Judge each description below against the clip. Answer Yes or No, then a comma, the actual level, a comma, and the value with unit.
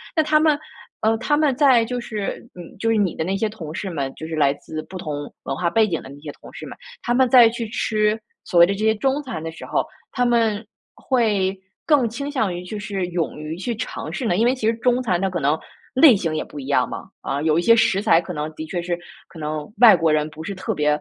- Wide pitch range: Yes, wide, 6.5 semitones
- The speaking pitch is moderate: No, high, 195 Hz